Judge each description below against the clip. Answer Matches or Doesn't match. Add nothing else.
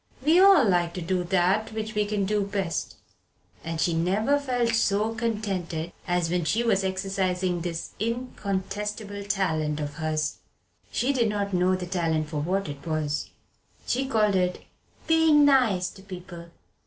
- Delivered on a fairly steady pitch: Doesn't match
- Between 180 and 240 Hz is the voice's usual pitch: Matches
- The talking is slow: Doesn't match